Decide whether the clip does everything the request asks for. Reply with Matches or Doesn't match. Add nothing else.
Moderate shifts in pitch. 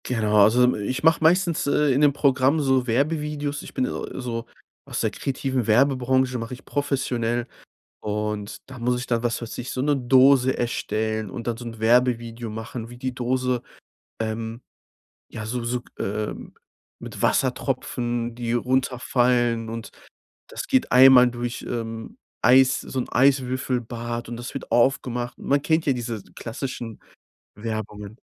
Doesn't match